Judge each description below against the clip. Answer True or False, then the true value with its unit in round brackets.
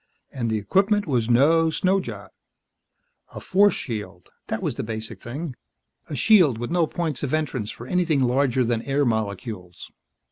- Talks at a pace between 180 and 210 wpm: False (165 wpm)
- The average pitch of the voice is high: False (130 Hz)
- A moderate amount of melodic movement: False (6.5 semitones)